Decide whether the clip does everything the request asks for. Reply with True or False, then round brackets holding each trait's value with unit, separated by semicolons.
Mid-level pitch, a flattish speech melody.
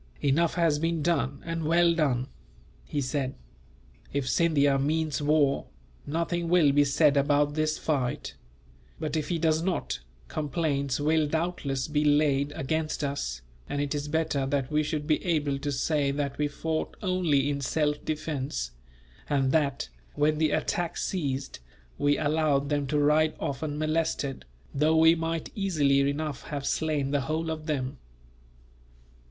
True (150 Hz; 2.2 semitones)